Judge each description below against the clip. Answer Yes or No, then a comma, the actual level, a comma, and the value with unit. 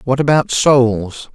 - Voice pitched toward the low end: Yes, low, 125 Hz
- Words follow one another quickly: No, slow, 135 wpm